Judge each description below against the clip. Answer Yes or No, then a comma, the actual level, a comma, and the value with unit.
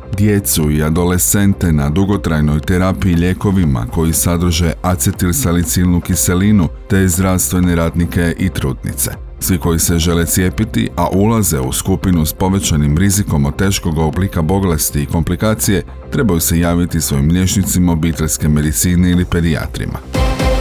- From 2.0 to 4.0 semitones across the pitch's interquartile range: Yes, narrow, 2.6 semitones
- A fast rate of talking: No, average, 125 wpm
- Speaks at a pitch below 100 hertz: Yes, very low, 90 Hz